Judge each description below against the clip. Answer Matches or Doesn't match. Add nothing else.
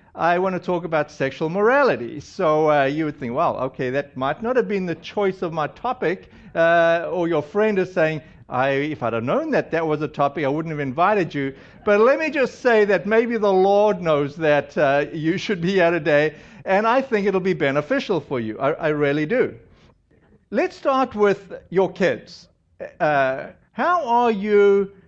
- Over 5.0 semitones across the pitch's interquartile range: Matches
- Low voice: Doesn't match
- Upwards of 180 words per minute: Matches